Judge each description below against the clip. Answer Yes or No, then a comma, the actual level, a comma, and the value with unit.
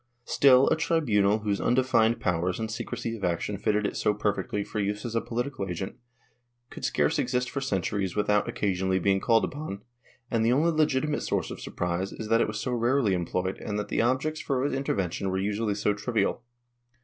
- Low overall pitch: Yes, low, 105 Hz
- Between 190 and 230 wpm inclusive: Yes, average, 195 wpm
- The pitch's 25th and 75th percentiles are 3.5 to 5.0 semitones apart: Yes, average, 4.2 semitones